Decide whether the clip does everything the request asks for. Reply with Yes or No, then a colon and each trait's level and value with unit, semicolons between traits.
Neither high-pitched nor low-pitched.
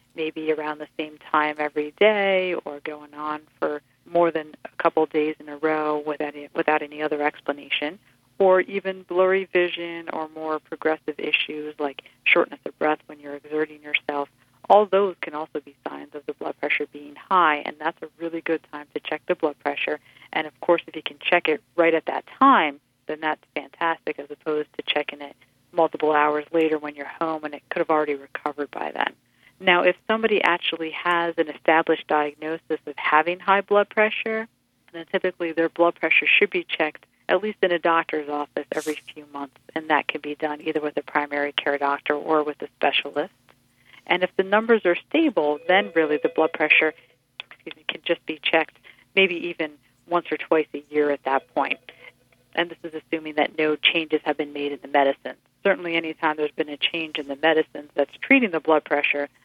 Yes: medium, 155 Hz